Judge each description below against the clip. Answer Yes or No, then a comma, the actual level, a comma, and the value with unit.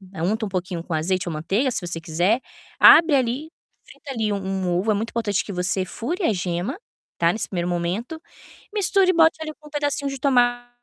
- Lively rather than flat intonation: Yes, wide, 7.3 semitones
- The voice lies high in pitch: Yes, high, 215 Hz